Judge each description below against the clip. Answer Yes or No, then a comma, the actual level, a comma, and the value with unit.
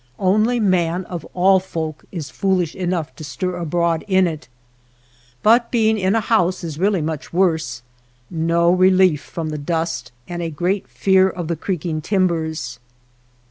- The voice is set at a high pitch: No, medium, 175 Hz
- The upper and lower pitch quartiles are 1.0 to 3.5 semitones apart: Yes, average, 2.9 semitones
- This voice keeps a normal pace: Yes, average, 160 wpm